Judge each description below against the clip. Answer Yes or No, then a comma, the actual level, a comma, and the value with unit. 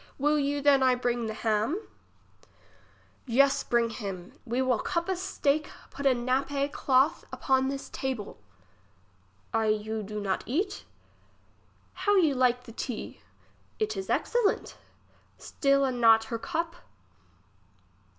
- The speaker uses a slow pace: Yes, slow, 130 wpm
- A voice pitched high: Yes, very high, 260 Hz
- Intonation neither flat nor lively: Yes, average, 3.9 semitones